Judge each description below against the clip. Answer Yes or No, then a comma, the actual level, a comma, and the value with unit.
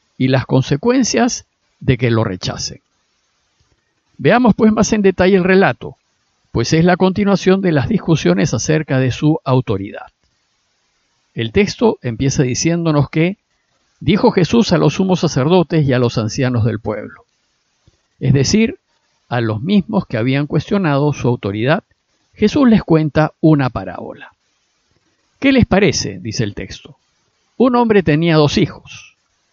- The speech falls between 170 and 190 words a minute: No, average, 140 wpm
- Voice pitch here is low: No, medium, 155 Hz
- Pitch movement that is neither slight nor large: No, wide, 7.0 semitones